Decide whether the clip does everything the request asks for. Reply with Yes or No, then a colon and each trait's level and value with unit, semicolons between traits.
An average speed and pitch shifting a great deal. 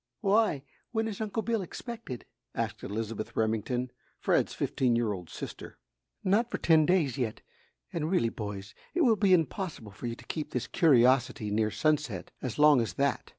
Yes: average, 170 wpm; wide, 8.8 semitones